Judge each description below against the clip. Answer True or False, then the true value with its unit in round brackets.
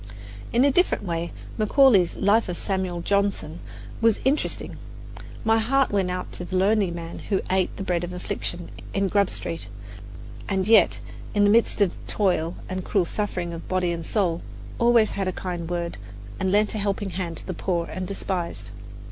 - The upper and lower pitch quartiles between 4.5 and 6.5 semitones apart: False (2.9 semitones)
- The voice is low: False (190 Hz)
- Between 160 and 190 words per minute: True (180 wpm)